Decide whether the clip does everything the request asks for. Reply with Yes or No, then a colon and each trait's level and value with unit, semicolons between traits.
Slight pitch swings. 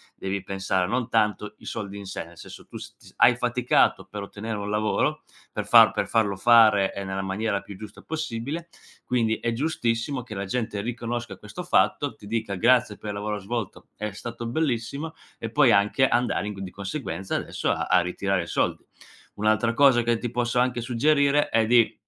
No: average, 3.3 semitones